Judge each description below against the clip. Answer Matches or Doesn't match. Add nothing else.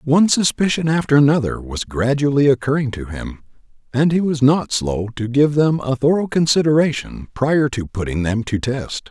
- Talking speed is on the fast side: Doesn't match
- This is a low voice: Matches